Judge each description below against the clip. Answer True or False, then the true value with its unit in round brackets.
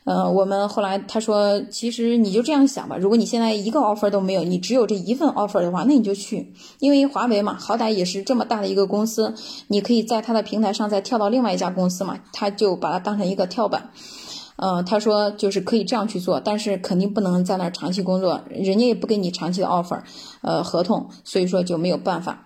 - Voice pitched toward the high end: True (205 Hz)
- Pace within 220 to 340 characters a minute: False (380 characters per minute)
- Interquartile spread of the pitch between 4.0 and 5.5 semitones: False (3.1 semitones)